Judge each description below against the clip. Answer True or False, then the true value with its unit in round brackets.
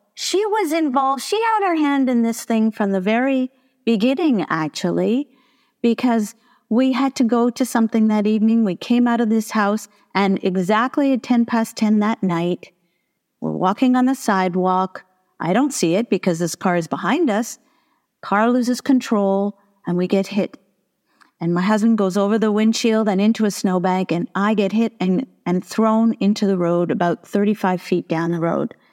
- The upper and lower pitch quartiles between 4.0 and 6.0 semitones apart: True (4.6 semitones)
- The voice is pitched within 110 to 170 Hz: False (215 Hz)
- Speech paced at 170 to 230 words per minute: True (180 wpm)